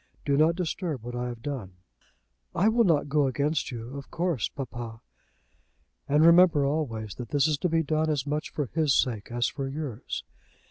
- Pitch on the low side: No, medium, 145 Hz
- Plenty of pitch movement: No, average, 4.5 semitones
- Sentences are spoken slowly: No, average, 185 wpm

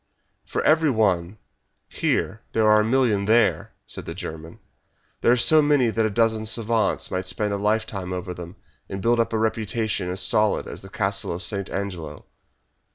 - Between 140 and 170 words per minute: No, average, 180 wpm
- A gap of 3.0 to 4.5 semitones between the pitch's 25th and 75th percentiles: Yes, average, 3.3 semitones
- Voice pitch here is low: Yes, low, 105 Hz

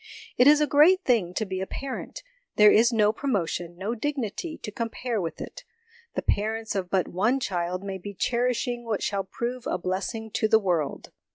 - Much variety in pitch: No, average, 4.4 semitones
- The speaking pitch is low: No, high, 220 Hz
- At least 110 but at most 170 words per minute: No, average, 190 wpm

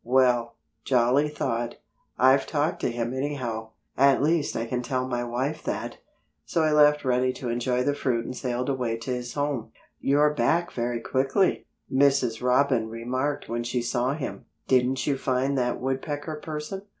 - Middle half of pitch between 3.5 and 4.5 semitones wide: No, average, 2.9 semitones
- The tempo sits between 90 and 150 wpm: No, average, 165 wpm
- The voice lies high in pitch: No, low, 130 Hz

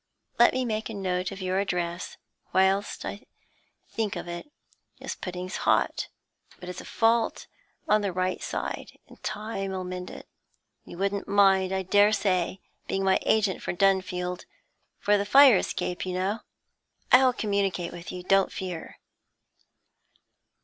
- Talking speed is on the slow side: No, average, 150 wpm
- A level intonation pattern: Yes, narrow, 2.1 semitones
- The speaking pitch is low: No, high, 190 Hz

